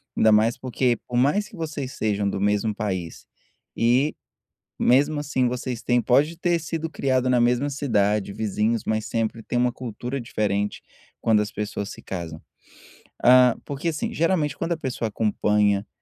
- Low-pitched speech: Yes, low, 120 Hz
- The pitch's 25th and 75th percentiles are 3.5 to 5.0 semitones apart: Yes, average, 4.7 semitones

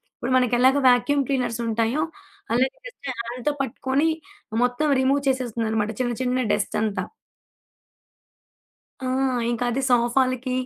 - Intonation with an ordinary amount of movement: No, narrow, 2.0 semitones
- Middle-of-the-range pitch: No, very high, 250 Hz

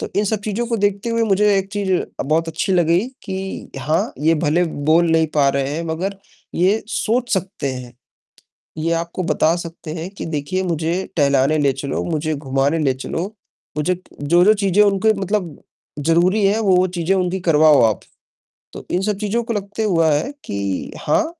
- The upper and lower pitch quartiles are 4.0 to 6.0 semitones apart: Yes, average, 4.4 semitones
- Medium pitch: Yes, medium, 175 Hz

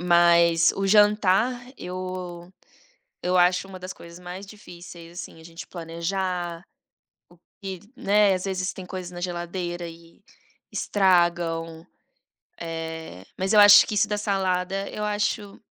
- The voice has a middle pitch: Yes, medium, 180 Hz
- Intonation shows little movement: Yes, narrow, 2.2 semitones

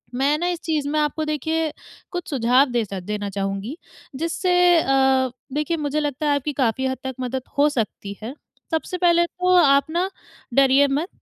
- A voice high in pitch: Yes, very high, 290 Hz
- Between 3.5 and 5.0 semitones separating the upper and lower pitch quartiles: Yes, average, 4.0 semitones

